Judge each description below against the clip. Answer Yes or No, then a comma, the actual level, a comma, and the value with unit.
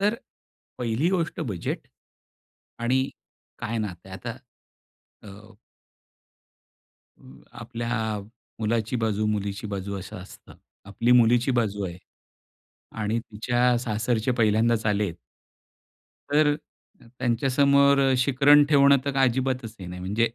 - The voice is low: Yes, low, 115 Hz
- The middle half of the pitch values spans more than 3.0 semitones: Yes, average, 3.5 semitones